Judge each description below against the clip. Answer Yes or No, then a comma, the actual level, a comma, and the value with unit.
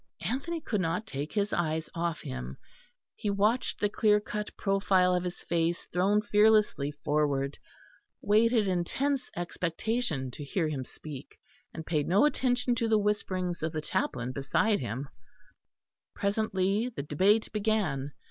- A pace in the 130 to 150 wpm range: Yes, average, 145 wpm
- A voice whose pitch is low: No, medium, 185 Hz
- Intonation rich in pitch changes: Yes, wide, 5.8 semitones